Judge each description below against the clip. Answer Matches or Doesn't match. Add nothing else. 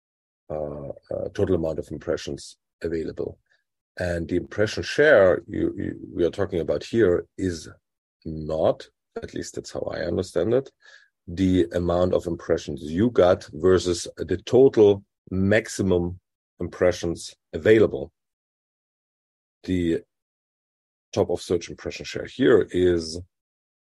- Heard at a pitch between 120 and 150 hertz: Doesn't match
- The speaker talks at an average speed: Doesn't match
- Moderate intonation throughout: Doesn't match